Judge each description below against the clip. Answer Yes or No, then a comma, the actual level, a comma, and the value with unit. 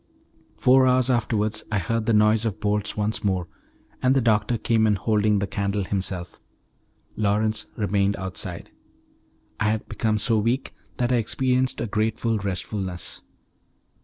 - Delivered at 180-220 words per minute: No, average, 145 wpm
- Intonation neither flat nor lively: No, narrow, 2.2 semitones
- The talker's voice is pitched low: Yes, low, 105 Hz